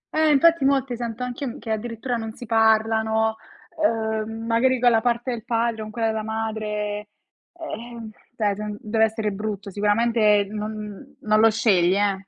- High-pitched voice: Yes, high, 220 Hz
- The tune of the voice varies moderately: No, narrow, 1.7 semitones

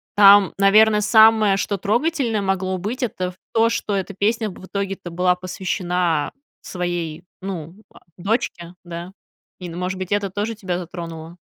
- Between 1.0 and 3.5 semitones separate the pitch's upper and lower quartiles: Yes, average, 2.8 semitones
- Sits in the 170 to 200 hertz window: Yes, high, 190 Hz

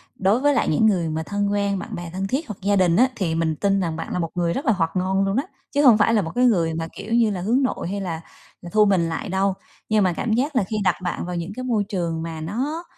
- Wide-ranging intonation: No, average, 4.4 semitones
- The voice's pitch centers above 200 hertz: No, high, 195 Hz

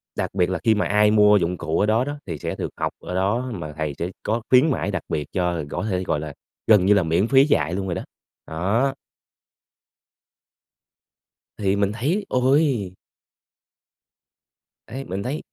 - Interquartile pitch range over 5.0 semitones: Yes, wide, 5.6 semitones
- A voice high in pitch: No, low, 100 Hz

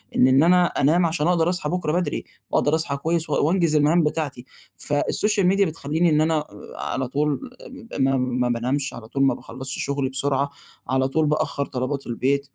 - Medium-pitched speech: Yes, medium, 145 Hz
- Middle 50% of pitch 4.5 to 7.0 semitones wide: No, average, 3.4 semitones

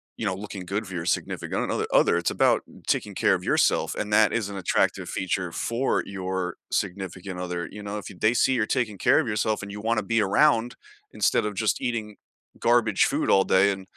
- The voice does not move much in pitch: No, average, 3.0 semitones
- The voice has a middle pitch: No, low, 100 Hz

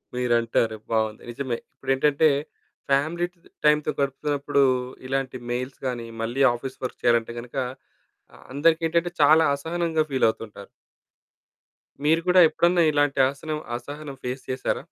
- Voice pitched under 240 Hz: Yes, medium, 140 Hz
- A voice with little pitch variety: No, average, 3.8 semitones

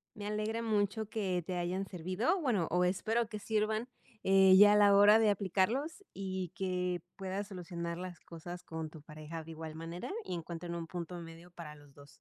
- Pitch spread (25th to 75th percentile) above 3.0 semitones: Yes, average, 3.5 semitones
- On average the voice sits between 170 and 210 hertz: Yes, medium, 185 Hz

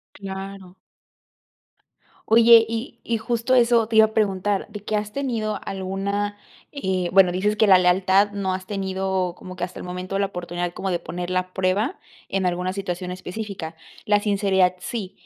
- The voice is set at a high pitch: Yes, high, 195 Hz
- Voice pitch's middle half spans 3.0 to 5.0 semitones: No, narrow, 2.5 semitones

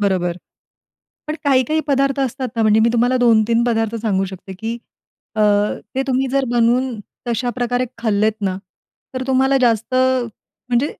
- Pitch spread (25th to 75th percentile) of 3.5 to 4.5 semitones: No, average, 2.8 semitones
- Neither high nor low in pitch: No, high, 240 Hz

